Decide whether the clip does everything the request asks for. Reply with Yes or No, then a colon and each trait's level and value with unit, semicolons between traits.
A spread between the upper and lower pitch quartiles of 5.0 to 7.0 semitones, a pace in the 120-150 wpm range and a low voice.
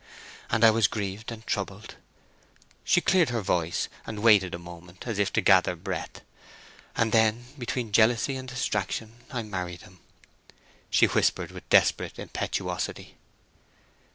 No: average, 3.7 semitones; average, 140 wpm; low, 110 Hz